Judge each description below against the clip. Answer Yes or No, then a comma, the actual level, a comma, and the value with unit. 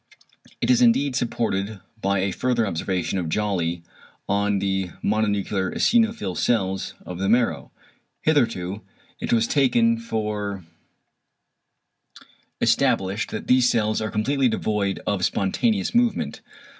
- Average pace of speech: No, slow, 120 wpm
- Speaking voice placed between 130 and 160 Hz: No, low, 105 Hz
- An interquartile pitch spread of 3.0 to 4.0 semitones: No, average, 4.6 semitones